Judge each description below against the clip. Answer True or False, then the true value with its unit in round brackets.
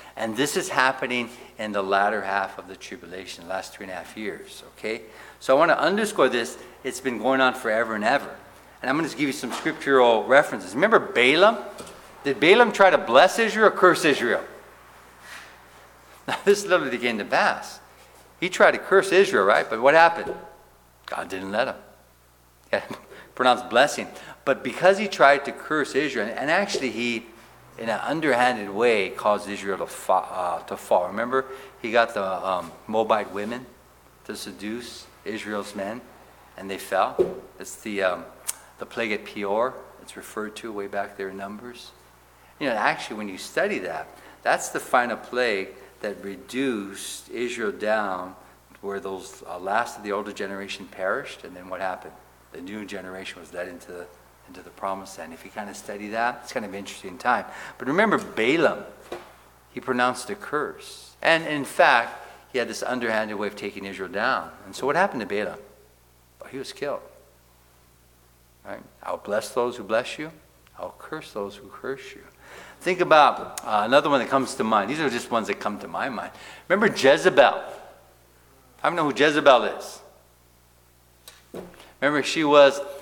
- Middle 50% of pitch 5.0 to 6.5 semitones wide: True (5.4 semitones)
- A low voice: True (105 Hz)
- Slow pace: False (180 wpm)